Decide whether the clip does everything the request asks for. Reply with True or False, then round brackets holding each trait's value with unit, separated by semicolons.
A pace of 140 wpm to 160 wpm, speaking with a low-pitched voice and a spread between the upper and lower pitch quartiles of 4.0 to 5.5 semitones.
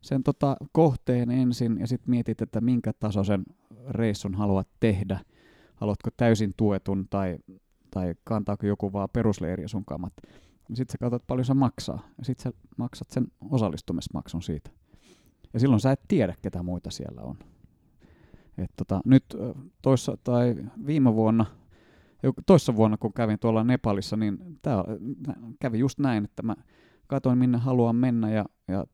True (150 wpm; 115 Hz; 4.3 semitones)